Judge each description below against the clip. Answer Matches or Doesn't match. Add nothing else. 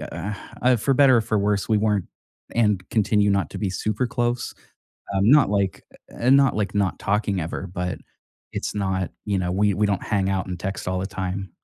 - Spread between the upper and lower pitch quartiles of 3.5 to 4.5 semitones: Doesn't match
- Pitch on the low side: Matches